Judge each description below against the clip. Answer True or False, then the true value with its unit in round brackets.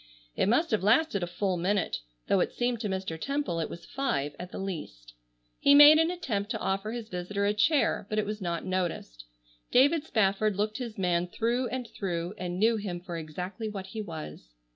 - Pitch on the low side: False (200 Hz)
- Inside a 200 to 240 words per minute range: True (205 wpm)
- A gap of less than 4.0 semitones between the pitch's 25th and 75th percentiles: False (4.6 semitones)